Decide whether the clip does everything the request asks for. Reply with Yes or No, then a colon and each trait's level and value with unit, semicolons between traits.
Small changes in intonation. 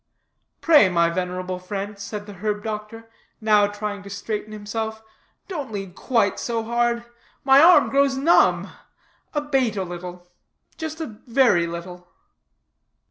No: average, 3.7 semitones